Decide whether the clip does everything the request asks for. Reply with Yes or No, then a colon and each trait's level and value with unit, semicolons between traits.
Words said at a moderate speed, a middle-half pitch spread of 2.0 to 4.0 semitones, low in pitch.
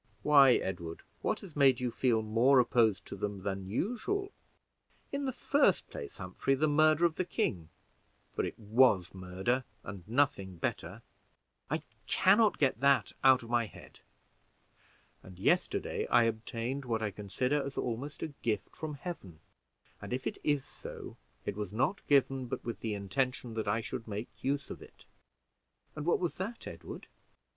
No: average, 170 wpm; wide, 5.5 semitones; low, 125 Hz